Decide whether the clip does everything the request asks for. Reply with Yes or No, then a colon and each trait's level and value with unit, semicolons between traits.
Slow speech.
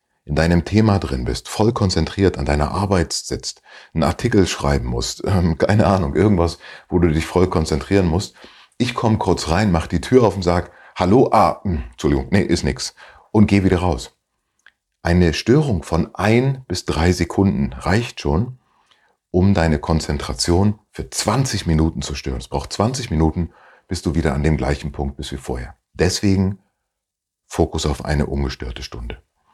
No: average, 170 wpm